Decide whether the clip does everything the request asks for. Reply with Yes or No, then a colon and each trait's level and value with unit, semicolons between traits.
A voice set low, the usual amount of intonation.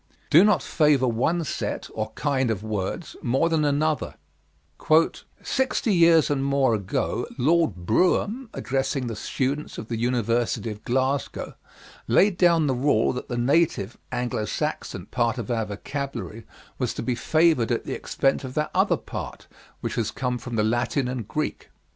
Yes: low, 130 Hz; average, 4.8 semitones